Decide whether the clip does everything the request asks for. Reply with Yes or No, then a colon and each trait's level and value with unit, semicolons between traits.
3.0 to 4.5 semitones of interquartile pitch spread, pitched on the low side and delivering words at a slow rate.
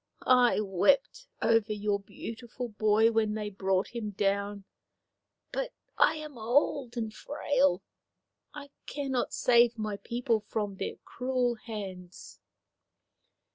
No: average, 3.4 semitones; high, 225 Hz; slow, 115 wpm